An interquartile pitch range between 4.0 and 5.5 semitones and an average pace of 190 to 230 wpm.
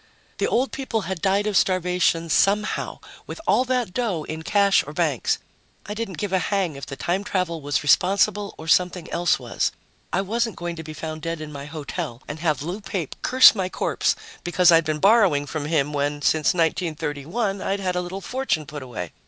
Yes: average, 4.4 semitones; average, 200 wpm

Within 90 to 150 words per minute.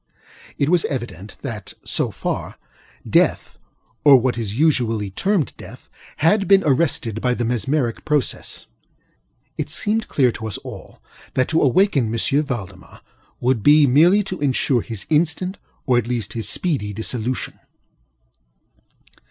Yes: slow, 135 wpm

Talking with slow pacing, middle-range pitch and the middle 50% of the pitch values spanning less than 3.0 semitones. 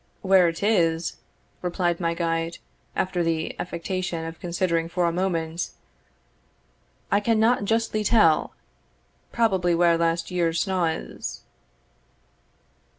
Yes: slow, 110 wpm; medium, 175 Hz; narrow, 2.4 semitones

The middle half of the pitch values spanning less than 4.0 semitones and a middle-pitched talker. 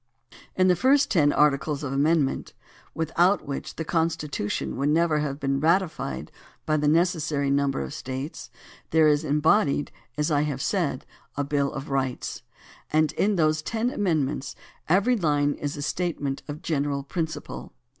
Yes: average, 2.8 semitones; medium, 150 Hz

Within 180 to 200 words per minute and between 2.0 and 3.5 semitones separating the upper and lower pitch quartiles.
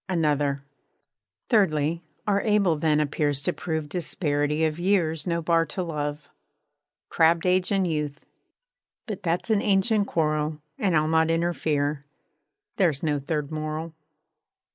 No: average, 140 wpm; average, 2.9 semitones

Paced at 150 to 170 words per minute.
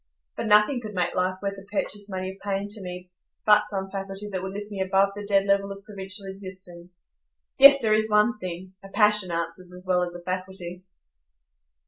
No: average, 195 wpm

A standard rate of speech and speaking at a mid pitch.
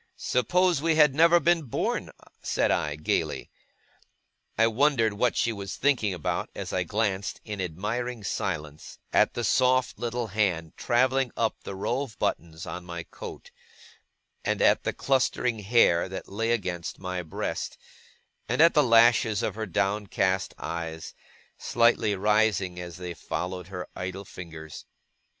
No: average, 145 wpm; low, 105 Hz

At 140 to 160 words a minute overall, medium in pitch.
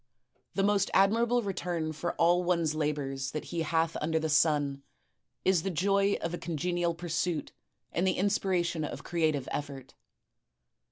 Yes: average, 155 wpm; medium, 170 Hz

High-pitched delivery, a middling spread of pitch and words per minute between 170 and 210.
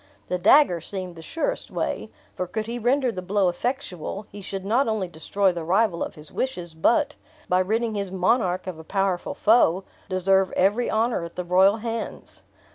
Yes: high, 195 Hz; average, 4.0 semitones; average, 185 wpm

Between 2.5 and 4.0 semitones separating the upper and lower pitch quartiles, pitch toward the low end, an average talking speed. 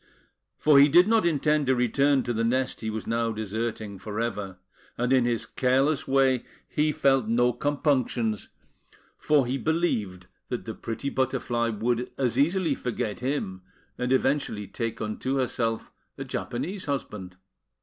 Yes: average, 3.7 semitones; low, 125 Hz; average, 150 wpm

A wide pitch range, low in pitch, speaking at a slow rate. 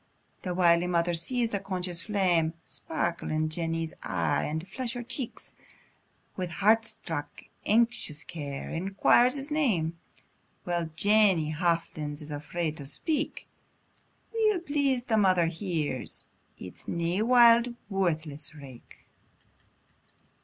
No: wide, 5.9 semitones; medium, 175 Hz; slow, 115 wpm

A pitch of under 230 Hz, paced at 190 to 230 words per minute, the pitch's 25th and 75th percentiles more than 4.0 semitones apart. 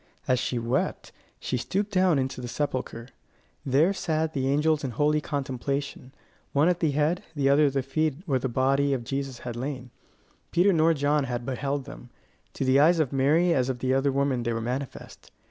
No: medium, 140 Hz; average, 195 wpm; average, 2.8 semitones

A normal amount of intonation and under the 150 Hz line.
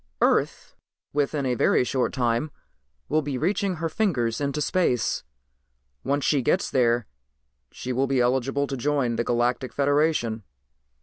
Yes: average, 3.3 semitones; low, 135 Hz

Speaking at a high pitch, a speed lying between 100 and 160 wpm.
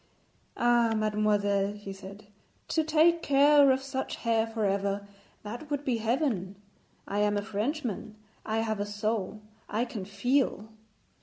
Yes: high, 220 Hz; average, 145 wpm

